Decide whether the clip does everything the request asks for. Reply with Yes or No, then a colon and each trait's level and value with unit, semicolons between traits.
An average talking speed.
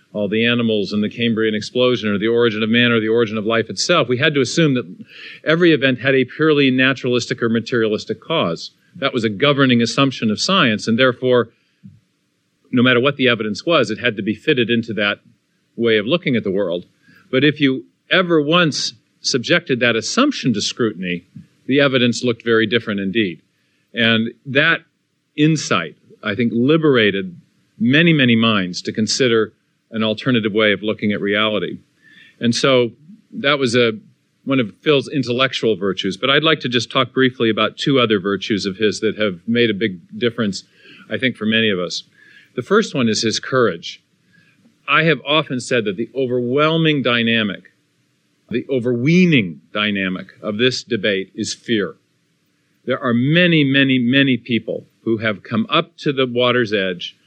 Yes: average, 175 wpm